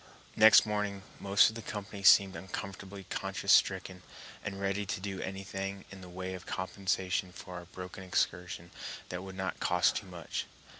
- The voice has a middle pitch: No, very low, 95 Hz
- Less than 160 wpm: No, average, 170 wpm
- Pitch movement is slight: Yes, narrow, 1.4 semitones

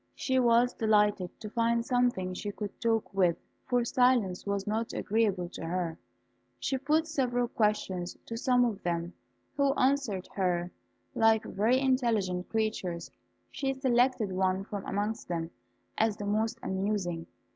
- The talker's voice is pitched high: Yes, high, 215 Hz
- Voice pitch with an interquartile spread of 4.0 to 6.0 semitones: Yes, average, 4.6 semitones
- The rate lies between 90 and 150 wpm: Yes, average, 145 wpm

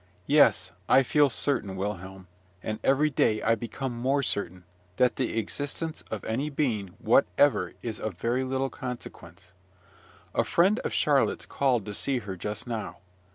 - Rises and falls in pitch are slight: No, average, 4.6 semitones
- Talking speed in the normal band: Yes, average, 155 wpm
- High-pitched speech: No, low, 120 Hz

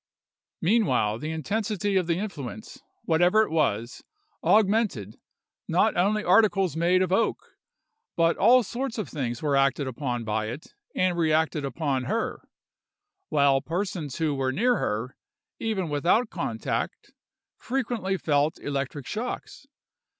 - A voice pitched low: No, medium, 165 Hz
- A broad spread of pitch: Yes, wide, 6.9 semitones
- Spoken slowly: Yes, slow, 130 wpm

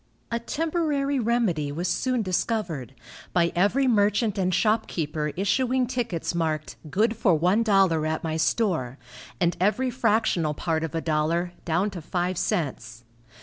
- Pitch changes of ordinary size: No, wide, 6.1 semitones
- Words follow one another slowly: No, average, 145 wpm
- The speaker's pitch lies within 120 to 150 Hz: No, medium, 185 Hz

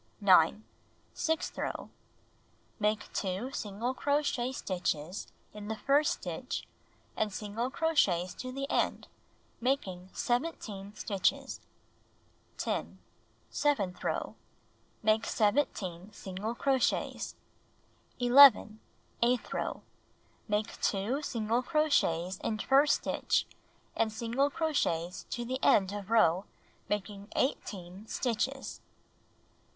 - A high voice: Yes, high, 220 Hz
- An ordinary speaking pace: No, slow, 100 wpm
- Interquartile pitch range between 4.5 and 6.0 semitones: Yes, average, 5.1 semitones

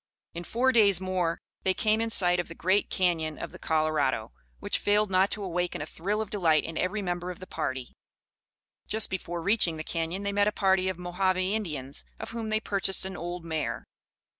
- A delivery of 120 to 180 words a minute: No, fast, 205 wpm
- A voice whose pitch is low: No, medium, 185 Hz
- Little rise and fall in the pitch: No, average, 3.4 semitones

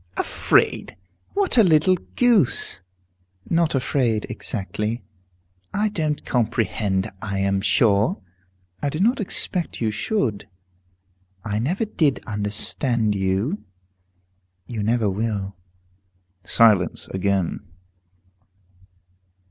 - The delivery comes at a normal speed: No, slow, 90 wpm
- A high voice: No, low, 115 Hz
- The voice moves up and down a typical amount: No, wide, 7.5 semitones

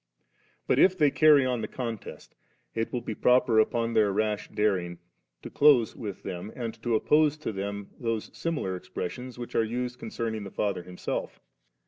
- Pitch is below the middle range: Yes, low, 115 Hz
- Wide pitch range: No, average, 3.6 semitones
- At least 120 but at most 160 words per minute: No, average, 170 wpm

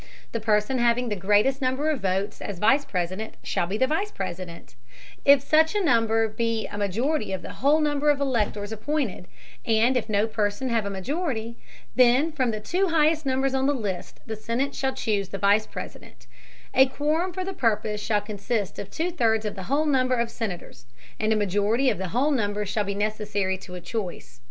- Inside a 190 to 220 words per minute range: Yes, average, 200 wpm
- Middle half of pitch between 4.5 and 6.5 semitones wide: Yes, average, 4.8 semitones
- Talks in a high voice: Yes, high, 225 Hz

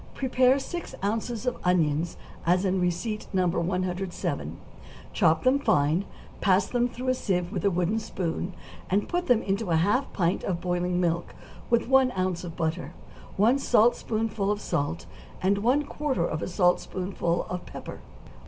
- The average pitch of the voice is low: No, high, 190 Hz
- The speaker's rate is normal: Yes, average, 160 wpm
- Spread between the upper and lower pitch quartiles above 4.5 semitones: Yes, average, 5.0 semitones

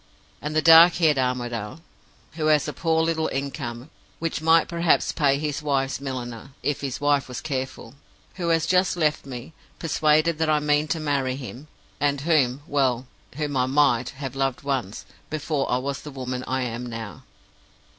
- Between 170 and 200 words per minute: Yes, average, 175 wpm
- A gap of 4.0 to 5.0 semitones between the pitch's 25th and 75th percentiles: No, average, 3.2 semitones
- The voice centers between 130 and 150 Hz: Yes, medium, 140 Hz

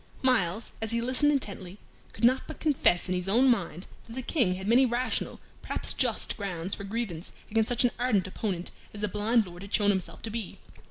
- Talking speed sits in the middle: No, fast, 210 wpm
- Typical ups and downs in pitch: Yes, average, 4.5 semitones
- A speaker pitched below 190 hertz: No, high, 215 Hz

